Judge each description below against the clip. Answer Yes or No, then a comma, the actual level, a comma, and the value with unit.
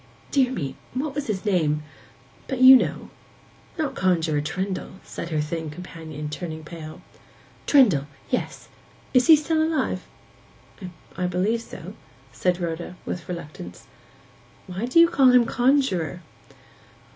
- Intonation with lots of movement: Yes, wide, 8.1 semitones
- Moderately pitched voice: Yes, medium, 180 Hz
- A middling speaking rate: No, slow, 120 wpm